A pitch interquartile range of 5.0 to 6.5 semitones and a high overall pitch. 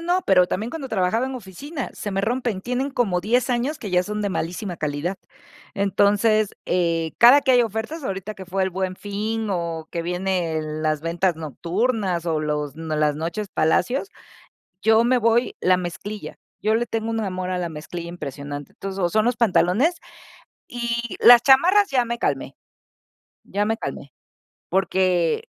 Yes: wide, 5.4 semitones; high, 195 Hz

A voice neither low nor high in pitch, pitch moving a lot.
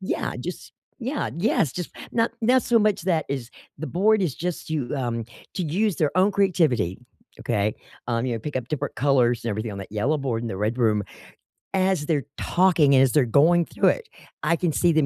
Yes: medium, 150 Hz; wide, 7.4 semitones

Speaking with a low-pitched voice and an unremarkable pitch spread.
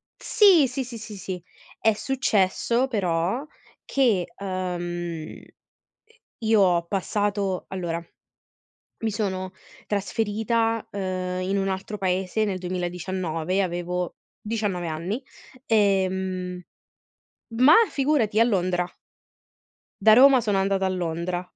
No: high, 190 Hz; average, 3.5 semitones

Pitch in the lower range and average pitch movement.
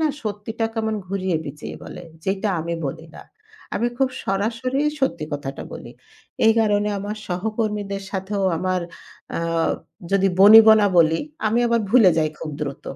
No: high, 200 Hz; average, 3.6 semitones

